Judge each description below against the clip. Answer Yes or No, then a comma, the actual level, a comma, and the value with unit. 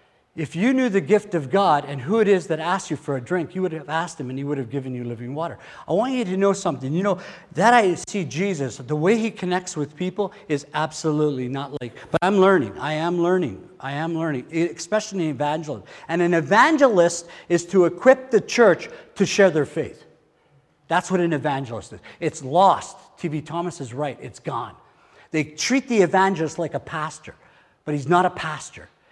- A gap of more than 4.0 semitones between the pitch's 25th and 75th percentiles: Yes, average, 4.6 semitones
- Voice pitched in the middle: Yes, medium, 170 Hz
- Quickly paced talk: Yes, fast, 210 wpm